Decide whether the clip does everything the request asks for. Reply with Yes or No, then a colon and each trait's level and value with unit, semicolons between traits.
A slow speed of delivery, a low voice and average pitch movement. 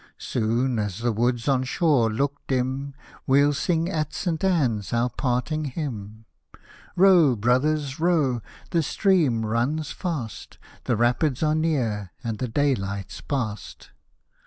Yes: slow, 130 wpm; low, 130 Hz; average, 4.9 semitones